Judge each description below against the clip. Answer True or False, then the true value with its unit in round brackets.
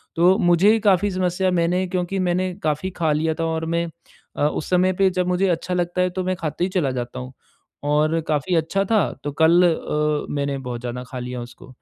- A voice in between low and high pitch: True (170 Hz)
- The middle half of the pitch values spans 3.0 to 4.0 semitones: True (3.6 semitones)